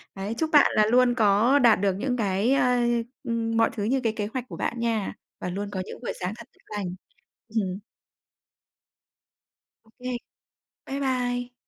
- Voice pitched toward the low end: No, high, 225 Hz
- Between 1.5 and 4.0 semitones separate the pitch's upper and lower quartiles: Yes, average, 3.4 semitones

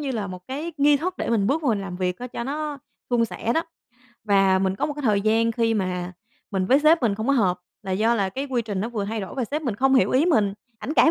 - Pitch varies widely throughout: Yes, wide, 5.7 semitones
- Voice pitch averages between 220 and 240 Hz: Yes, high, 230 Hz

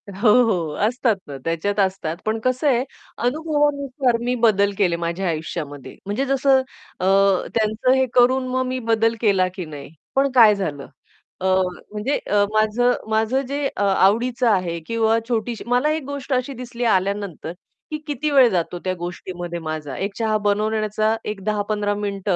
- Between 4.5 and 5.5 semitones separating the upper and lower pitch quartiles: Yes, average, 4.9 semitones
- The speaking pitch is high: Yes, high, 215 Hz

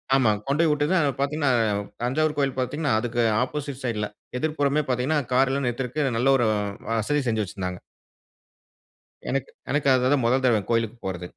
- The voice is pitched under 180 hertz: Yes, low, 135 Hz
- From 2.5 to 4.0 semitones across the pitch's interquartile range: Yes, average, 3.4 semitones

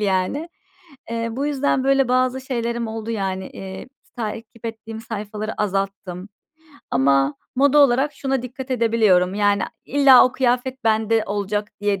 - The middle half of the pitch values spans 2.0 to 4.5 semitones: Yes, average, 4.1 semitones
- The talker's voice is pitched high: Yes, high, 225 Hz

